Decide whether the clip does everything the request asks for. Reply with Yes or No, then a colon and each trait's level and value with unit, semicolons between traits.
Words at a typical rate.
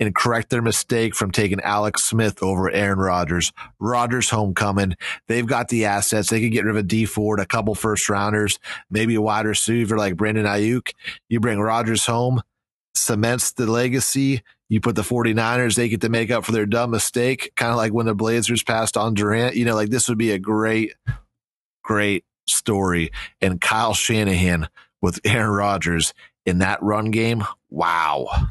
Yes: average, 180 wpm